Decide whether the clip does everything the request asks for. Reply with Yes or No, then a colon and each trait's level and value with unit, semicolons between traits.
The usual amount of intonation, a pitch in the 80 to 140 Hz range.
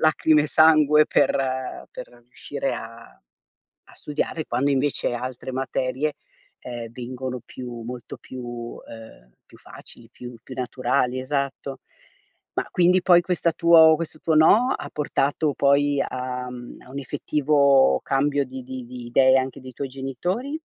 Yes: average, 3.3 semitones; low, 135 Hz